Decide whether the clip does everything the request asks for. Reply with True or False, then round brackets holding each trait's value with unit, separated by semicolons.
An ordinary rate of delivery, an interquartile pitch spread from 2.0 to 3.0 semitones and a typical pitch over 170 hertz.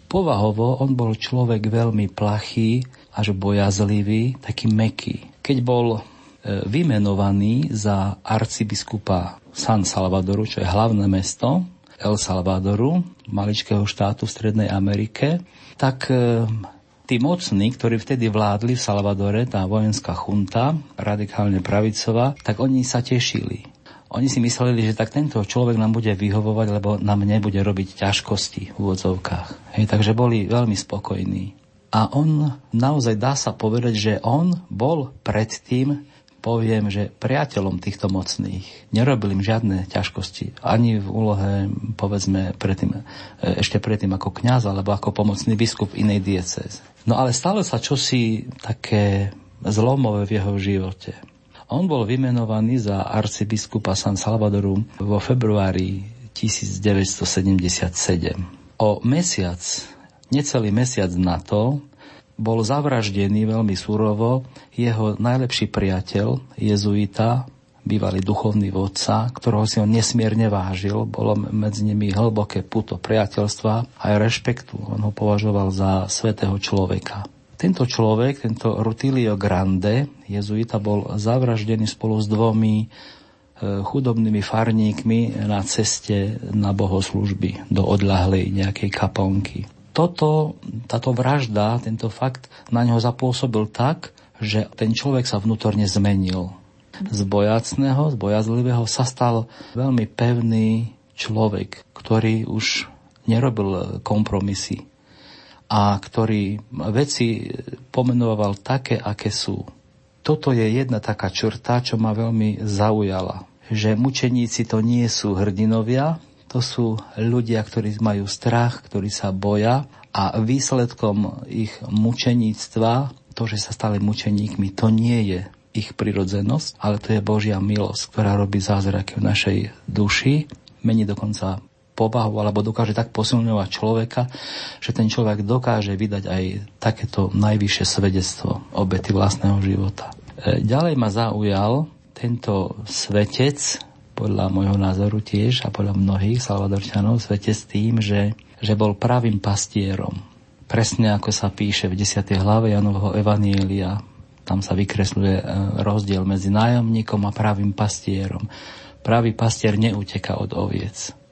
False (120 wpm; 2.7 semitones; 110 Hz)